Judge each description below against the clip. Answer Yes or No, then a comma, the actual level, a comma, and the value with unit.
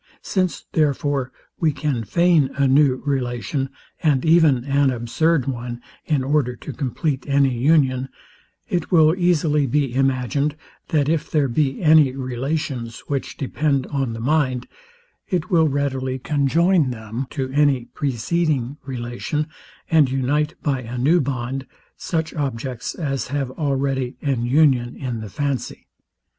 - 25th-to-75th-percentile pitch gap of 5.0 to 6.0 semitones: No, average, 2.9 semitones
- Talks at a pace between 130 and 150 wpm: Yes, slow, 135 wpm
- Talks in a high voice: No, medium, 140 Hz